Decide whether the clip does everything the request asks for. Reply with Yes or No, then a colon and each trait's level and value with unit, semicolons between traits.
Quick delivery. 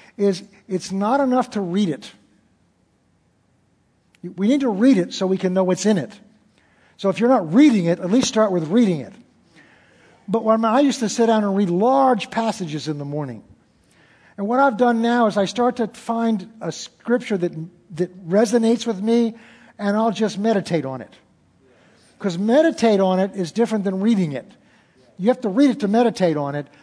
No: average, 190 wpm